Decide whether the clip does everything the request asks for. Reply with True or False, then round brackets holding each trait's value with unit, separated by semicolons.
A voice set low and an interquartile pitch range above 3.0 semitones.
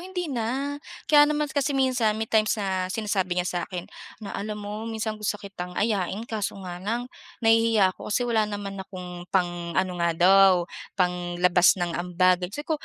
False (200 Hz; 3.9 semitones)